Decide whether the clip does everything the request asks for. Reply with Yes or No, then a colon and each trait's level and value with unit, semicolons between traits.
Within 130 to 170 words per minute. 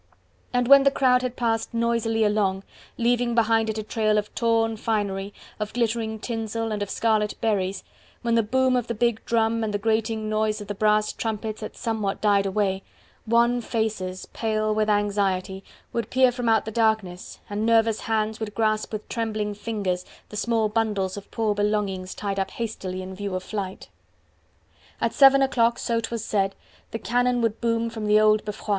No: average, 185 wpm